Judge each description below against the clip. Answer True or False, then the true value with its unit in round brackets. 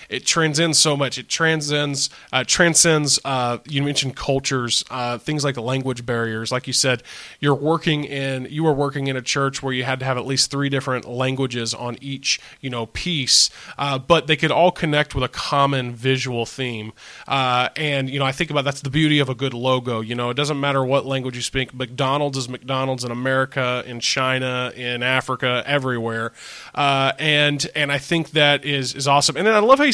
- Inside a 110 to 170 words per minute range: False (205 wpm)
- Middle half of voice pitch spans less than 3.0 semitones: True (2.4 semitones)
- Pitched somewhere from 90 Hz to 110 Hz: False (135 Hz)